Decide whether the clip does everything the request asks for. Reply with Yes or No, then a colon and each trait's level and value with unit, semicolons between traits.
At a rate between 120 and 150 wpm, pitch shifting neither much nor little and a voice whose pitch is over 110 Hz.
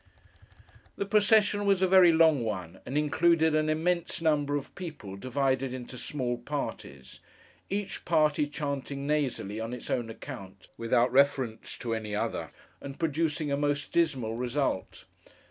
Yes: average, 145 wpm; average, 4.9 semitones; medium, 140 Hz